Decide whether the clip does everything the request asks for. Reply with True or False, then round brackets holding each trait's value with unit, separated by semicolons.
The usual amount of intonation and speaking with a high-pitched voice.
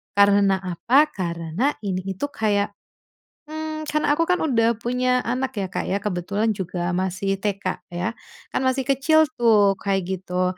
False (5.8 semitones; 205 Hz)